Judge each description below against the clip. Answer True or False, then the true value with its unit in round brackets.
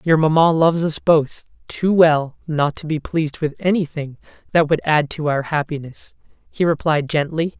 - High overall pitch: False (155 Hz)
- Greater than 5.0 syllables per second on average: False (4.8 syllables/s)